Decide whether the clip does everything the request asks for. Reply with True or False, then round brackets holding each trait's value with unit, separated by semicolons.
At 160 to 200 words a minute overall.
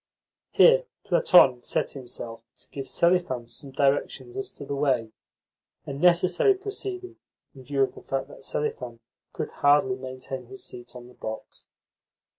False (150 wpm)